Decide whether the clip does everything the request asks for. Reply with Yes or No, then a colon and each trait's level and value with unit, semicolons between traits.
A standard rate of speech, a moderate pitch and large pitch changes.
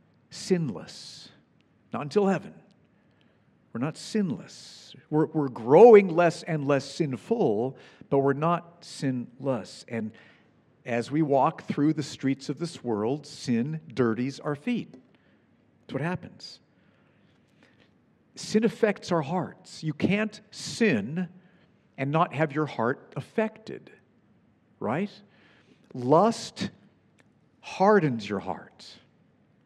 No: slow, 105 wpm; medium, 160 Hz; wide, 6.0 semitones